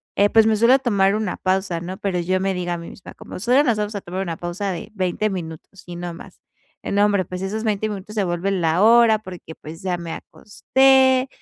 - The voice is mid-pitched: No, high, 195 Hz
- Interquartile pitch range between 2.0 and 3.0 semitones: No, average, 3.4 semitones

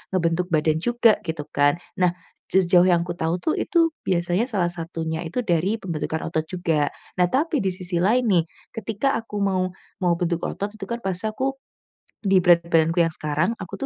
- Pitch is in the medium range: Yes, medium, 180 Hz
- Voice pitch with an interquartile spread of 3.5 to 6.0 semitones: Yes, average, 3.8 semitones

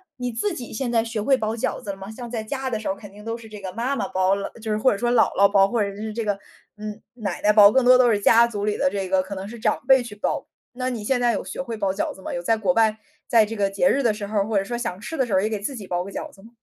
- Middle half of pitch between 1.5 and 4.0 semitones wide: Yes, average, 3.0 semitones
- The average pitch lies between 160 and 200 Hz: No, high, 215 Hz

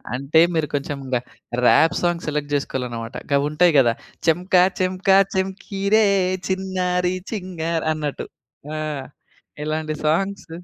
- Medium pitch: Yes, medium, 165 Hz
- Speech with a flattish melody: No, average, 4.1 semitones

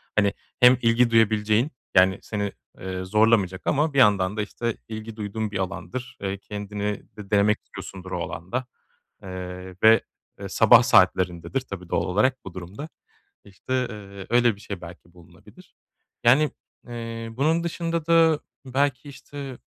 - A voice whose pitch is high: No, low, 105 Hz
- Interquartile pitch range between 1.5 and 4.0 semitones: No, average, 4.7 semitones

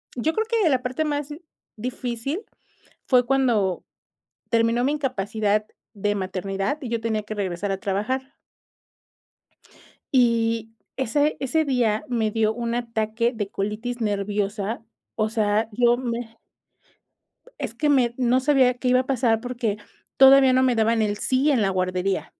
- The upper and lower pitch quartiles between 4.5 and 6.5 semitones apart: No, average, 3.4 semitones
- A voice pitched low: No, high, 230 Hz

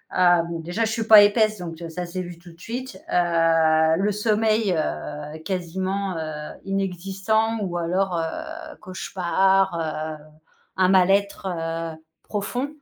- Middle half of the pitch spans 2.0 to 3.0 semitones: No, average, 3.7 semitones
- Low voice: No, medium, 185 Hz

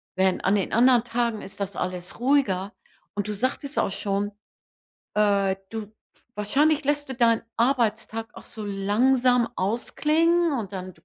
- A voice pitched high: Yes, high, 225 Hz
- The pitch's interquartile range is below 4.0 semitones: No, average, 4.5 semitones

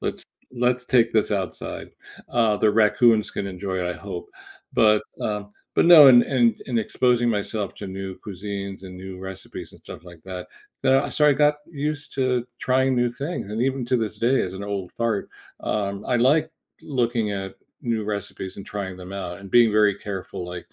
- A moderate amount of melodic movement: Yes, average, 4.3 semitones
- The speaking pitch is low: Yes, low, 110 Hz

